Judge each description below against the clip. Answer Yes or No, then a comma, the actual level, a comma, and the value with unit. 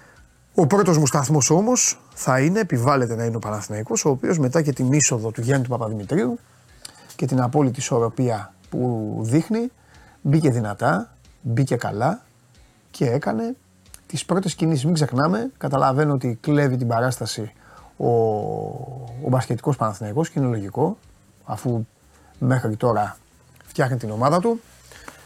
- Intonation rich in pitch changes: No, average, 5.0 semitones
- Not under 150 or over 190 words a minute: No, average, 140 wpm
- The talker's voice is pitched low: Yes, low, 130 Hz